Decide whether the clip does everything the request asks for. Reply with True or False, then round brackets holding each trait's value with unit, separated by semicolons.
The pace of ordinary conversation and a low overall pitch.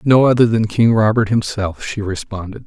True (180 wpm; 110 Hz)